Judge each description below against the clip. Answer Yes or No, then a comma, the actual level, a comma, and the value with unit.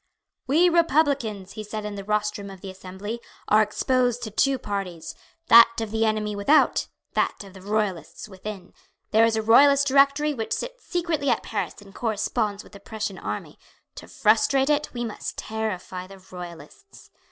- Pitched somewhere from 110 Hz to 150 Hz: No, high, 215 Hz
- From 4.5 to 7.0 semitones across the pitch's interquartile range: Yes, average, 4.8 semitones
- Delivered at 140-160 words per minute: No, average, 170 wpm